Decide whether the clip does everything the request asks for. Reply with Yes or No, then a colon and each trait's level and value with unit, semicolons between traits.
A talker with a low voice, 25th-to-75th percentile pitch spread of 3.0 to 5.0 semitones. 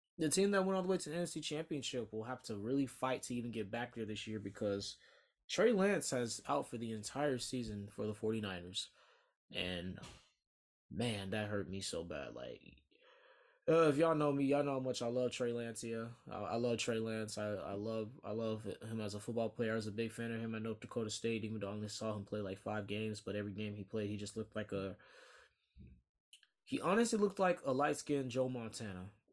Yes: low, 115 Hz; average, 4.0 semitones